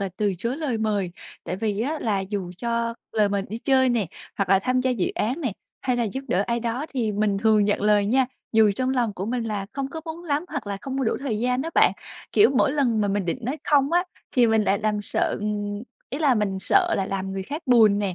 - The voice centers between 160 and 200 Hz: No, high, 225 Hz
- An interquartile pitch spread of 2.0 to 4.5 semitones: Yes, average, 4.2 semitones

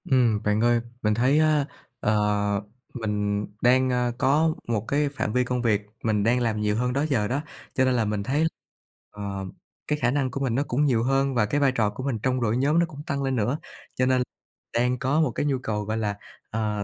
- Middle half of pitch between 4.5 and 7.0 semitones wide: No, average, 4.1 semitones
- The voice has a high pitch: No, low, 125 Hz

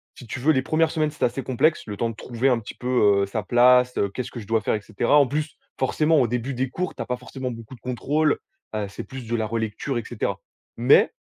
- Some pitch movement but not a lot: Yes, average, 3.1 semitones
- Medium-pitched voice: No, low, 125 Hz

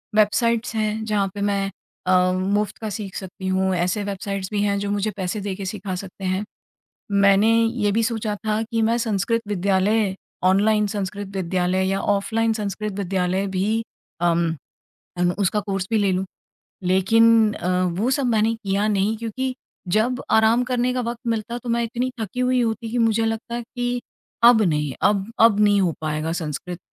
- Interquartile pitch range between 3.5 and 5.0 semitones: No, average, 3.0 semitones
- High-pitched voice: Yes, high, 205 Hz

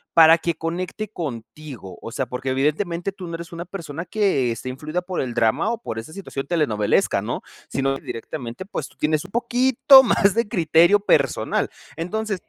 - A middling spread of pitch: No, wide, 6.3 semitones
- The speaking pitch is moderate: Yes, medium, 165 Hz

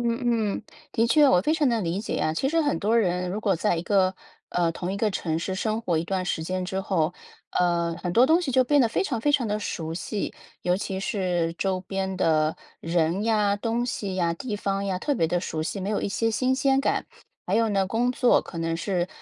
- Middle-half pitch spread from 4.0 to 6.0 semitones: Yes, average, 4.5 semitones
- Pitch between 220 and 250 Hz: No, high, 195 Hz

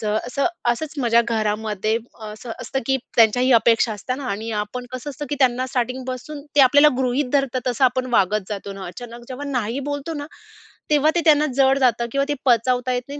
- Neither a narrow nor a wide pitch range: Yes, average, 3.3 semitones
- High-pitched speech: Yes, very high, 250 Hz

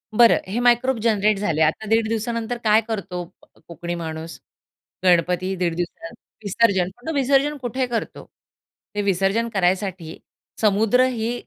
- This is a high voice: Yes, high, 210 Hz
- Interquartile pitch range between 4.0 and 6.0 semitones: Yes, average, 4.6 semitones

